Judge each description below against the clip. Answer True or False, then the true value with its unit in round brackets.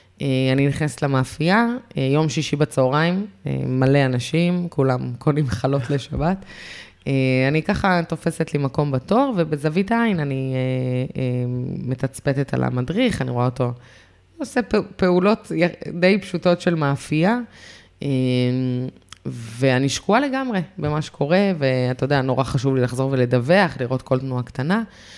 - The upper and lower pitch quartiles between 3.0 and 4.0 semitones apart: False (5.4 semitones)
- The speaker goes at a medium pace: True (135 wpm)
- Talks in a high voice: False (140 Hz)